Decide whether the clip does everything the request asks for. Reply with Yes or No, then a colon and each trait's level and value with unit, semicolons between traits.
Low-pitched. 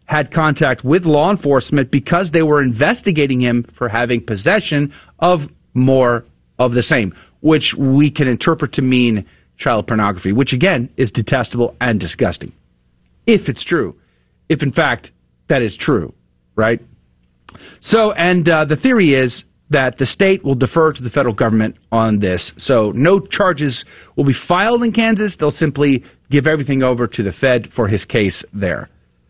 Yes: low, 130 Hz